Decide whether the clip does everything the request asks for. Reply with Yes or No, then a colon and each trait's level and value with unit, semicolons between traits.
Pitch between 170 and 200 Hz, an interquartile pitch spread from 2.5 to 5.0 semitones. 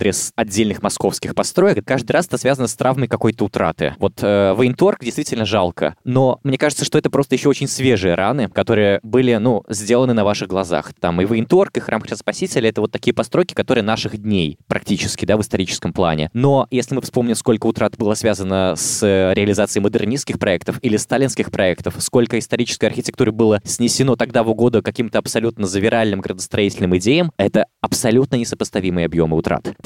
No: low, 115 Hz; average, 3.7 semitones